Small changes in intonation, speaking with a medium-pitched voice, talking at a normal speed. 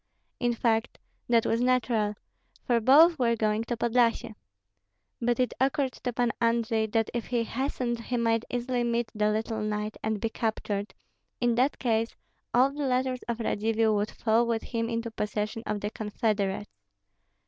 No: narrow, 1.9 semitones; high, 230 Hz; average, 165 wpm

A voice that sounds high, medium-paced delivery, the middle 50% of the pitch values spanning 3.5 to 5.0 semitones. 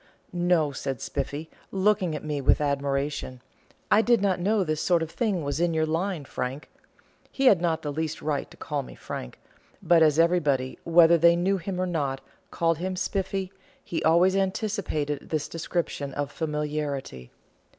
No: medium, 160 Hz; average, 170 wpm; average, 3.8 semitones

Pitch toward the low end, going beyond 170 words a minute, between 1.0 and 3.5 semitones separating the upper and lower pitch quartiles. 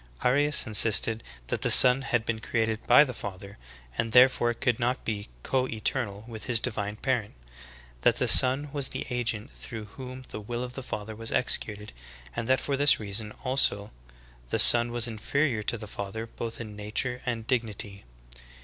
Yes: low, 115 Hz; average, 180 wpm; average, 3.1 semitones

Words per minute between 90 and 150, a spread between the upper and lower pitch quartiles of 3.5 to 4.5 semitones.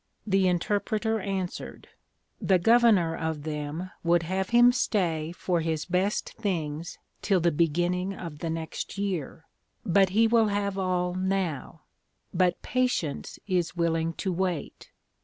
No: slow, 135 wpm; average, 3.1 semitones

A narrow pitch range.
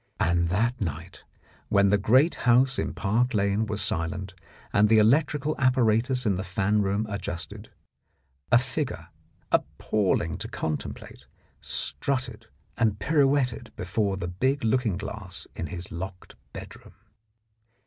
No: average, 5.0 semitones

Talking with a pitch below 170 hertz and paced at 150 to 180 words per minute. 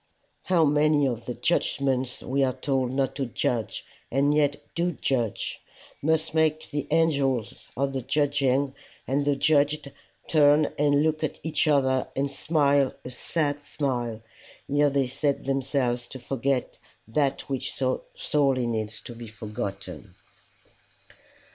No: medium, 140 Hz; average, 140 wpm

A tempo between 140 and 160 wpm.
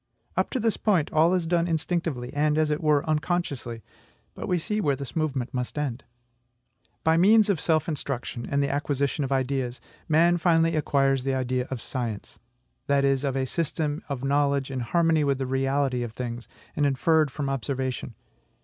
No: average, 175 wpm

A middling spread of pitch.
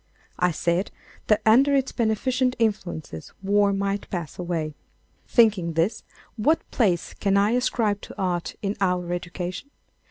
Yes: average, 4.1 semitones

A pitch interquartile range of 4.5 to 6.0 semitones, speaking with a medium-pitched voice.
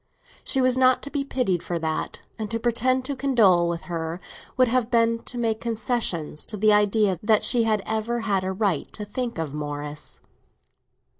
No: average, 5.1 semitones; high, 220 Hz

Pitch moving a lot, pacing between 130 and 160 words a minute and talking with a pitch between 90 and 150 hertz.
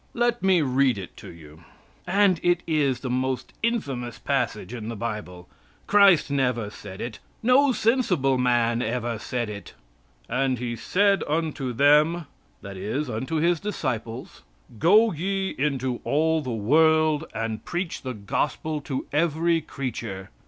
Yes: wide, 6.1 semitones; average, 145 wpm; low, 135 Hz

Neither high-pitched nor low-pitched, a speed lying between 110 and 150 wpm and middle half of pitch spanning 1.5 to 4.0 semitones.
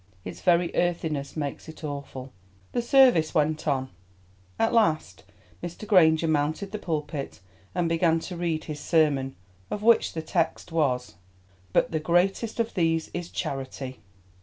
Yes: medium, 160 Hz; average, 145 wpm; average, 3.3 semitones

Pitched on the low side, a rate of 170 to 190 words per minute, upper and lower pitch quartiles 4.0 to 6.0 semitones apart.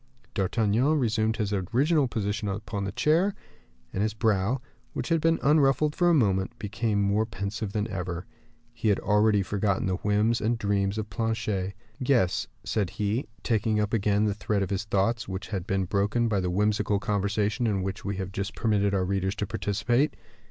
No: low, 105 Hz; average, 180 wpm; narrow, 2.5 semitones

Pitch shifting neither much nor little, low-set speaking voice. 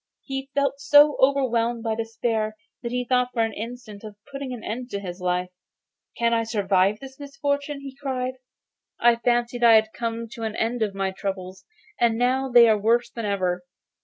No: average, 3.0 semitones; high, 235 Hz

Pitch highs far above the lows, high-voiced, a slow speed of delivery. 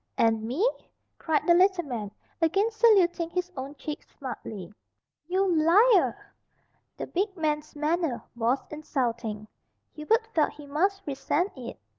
Yes: wide, 6.0 semitones; very high, 310 Hz; slow, 130 wpm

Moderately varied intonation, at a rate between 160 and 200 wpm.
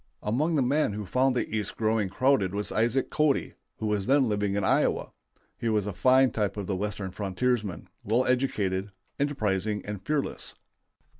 Yes: average, 4.1 semitones; average, 170 wpm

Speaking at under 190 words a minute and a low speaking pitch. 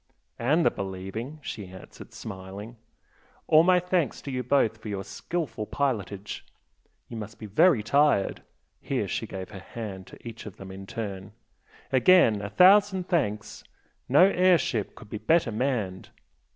Yes: average, 155 wpm; low, 115 Hz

